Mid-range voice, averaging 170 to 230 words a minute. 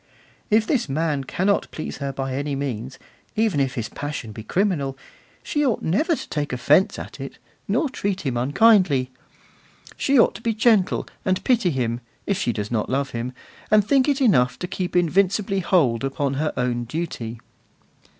Yes: medium, 150 Hz; average, 175 wpm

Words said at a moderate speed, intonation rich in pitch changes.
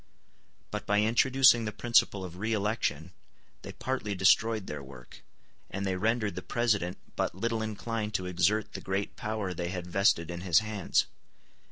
No: average, 165 wpm; average, 3.4 semitones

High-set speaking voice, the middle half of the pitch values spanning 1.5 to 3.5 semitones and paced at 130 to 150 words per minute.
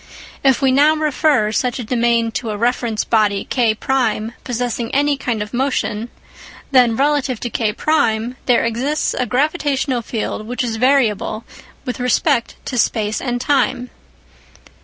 Yes: high, 245 Hz; average, 3.1 semitones; average, 140 wpm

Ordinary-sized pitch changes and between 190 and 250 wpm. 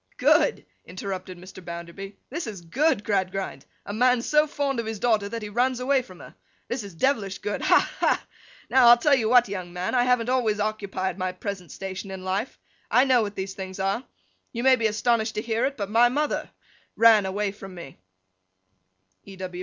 Yes: average, 4.2 semitones; average, 195 wpm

